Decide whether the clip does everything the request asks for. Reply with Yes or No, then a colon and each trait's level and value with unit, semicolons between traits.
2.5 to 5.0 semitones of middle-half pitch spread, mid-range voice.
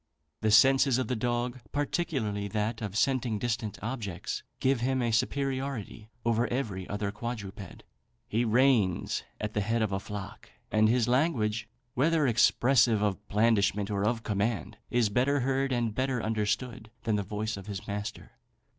No: average, 3.4 semitones; low, 115 Hz